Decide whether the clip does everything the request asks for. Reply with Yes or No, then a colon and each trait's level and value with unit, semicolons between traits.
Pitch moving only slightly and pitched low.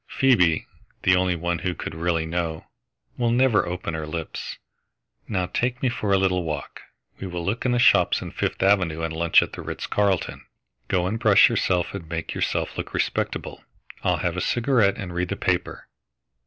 No: average, 3.5 semitones; very low, 90 Hz